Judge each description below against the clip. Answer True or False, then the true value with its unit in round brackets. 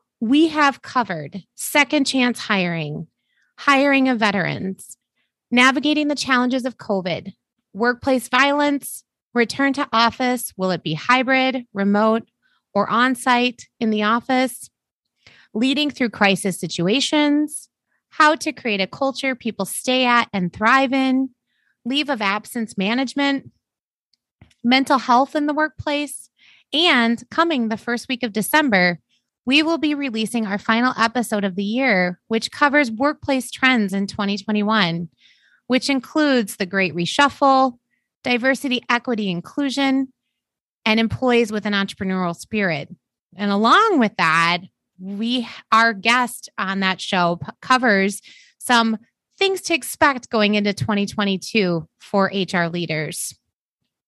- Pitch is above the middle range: True (240 Hz)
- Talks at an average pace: False (125 wpm)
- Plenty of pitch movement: False (5.0 semitones)